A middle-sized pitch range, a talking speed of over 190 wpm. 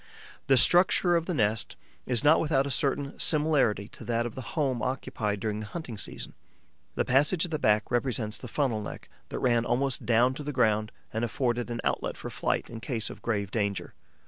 Yes: average, 4.2 semitones; average, 200 wpm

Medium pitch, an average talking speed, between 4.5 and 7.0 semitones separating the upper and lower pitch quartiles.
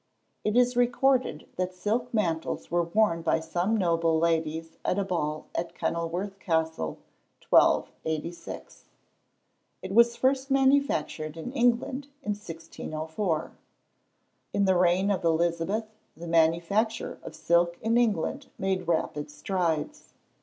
No: medium, 175 Hz; slow, 120 wpm; average, 5.1 semitones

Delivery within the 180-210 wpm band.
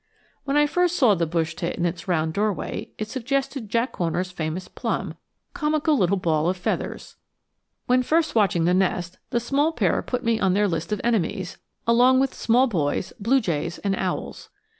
Yes: average, 185 wpm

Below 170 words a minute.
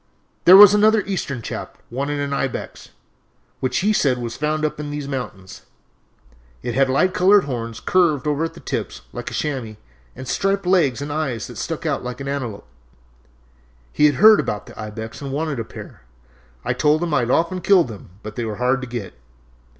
No: average, 195 wpm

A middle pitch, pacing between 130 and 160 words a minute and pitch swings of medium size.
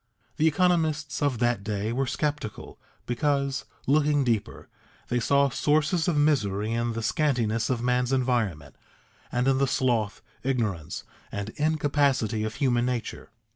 No: low, 125 Hz; slow, 135 wpm; average, 4.2 semitones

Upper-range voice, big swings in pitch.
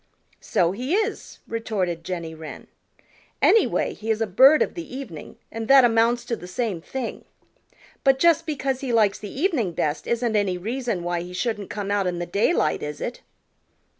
Yes: high, 225 Hz; wide, 6.3 semitones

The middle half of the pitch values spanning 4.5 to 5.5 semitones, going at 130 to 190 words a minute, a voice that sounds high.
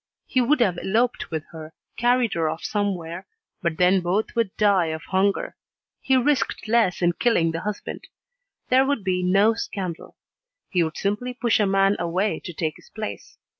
Yes: average, 4.9 semitones; average, 175 wpm; high, 195 Hz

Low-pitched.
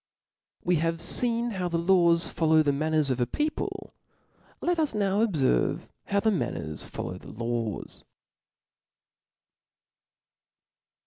No: medium, 170 Hz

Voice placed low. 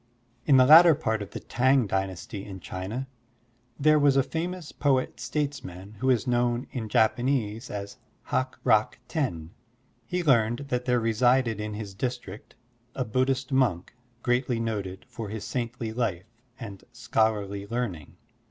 Yes: low, 120 Hz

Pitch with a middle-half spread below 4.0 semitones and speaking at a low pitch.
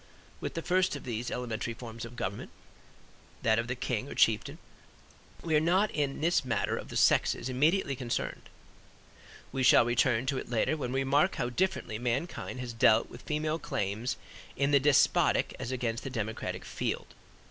No: average, 4.3 semitones; low, 130 Hz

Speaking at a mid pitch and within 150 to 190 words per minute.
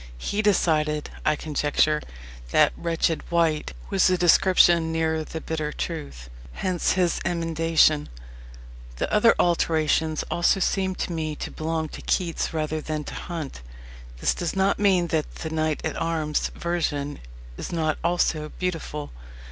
No: medium, 160 Hz; average, 140 wpm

